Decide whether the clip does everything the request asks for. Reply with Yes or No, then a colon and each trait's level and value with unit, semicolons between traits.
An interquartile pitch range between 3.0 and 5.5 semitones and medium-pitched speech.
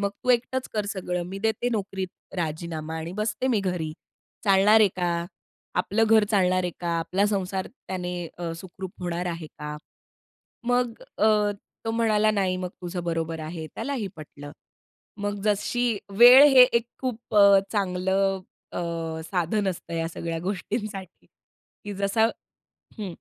No: average, 3.7 semitones; high, 195 Hz